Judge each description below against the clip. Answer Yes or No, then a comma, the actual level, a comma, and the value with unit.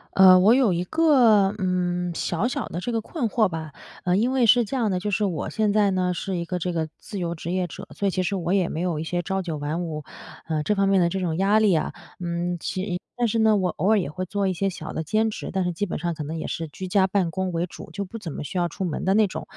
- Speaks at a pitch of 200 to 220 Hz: No, medium, 185 Hz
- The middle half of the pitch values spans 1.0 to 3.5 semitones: Yes, average, 3.1 semitones